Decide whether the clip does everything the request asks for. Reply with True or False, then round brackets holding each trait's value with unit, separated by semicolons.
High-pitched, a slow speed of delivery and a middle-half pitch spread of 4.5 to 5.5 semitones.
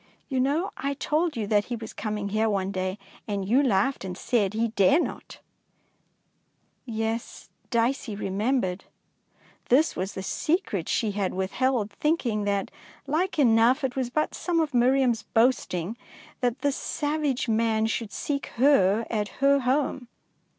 False (230 Hz; 150 wpm; 5.0 semitones)